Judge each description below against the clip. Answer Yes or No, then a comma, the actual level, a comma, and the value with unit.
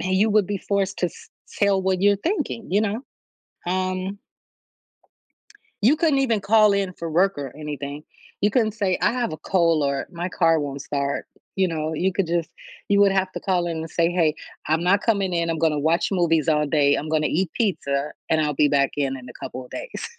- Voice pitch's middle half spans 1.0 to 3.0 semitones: No, average, 4.5 semitones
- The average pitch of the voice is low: No, medium, 175 Hz